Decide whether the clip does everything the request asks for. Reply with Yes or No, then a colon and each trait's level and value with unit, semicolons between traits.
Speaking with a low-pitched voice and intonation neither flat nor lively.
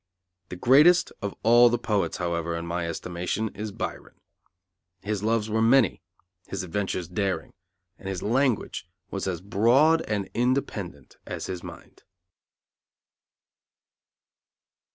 Yes: low, 100 Hz; average, 4.6 semitones